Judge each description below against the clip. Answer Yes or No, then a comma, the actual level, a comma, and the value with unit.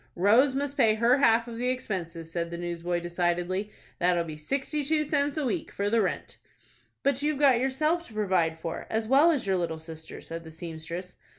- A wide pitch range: Yes, wide, 7.8 semitones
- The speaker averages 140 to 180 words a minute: No, average, 200 wpm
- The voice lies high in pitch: Yes, high, 205 Hz